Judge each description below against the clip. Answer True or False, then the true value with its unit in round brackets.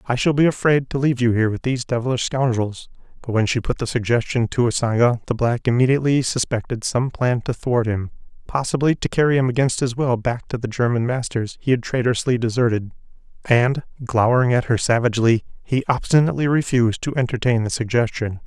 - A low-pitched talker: True (120 Hz)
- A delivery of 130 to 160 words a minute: False (180 wpm)